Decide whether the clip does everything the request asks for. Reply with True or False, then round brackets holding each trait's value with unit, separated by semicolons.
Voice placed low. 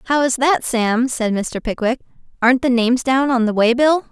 False (250 Hz)